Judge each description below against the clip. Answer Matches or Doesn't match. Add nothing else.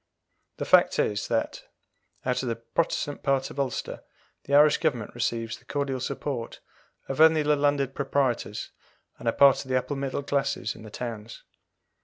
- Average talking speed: Matches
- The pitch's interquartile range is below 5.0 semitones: Matches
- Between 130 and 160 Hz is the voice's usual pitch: Matches